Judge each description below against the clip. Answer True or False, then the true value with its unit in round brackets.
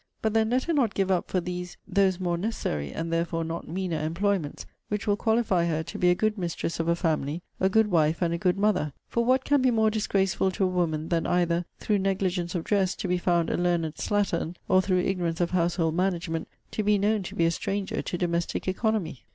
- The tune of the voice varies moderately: True (3.2 semitones)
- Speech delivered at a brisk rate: True (225 wpm)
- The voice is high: False (180 Hz)